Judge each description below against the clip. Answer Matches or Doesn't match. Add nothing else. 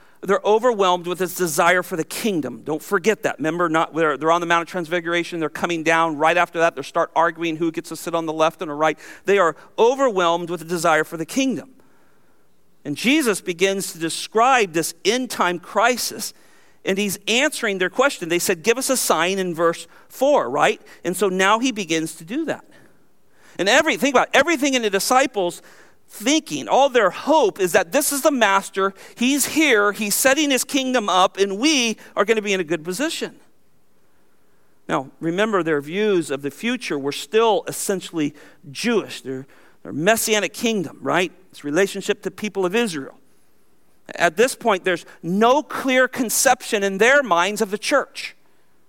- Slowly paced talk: Doesn't match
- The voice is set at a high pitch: Matches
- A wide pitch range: Matches